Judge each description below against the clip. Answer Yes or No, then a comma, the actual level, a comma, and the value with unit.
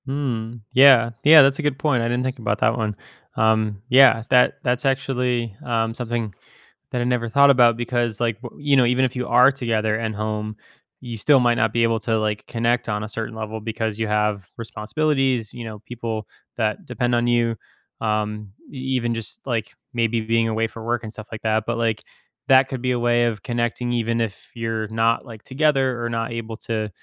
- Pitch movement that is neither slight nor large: No, narrow, 2.0 semitones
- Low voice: Yes, low, 115 Hz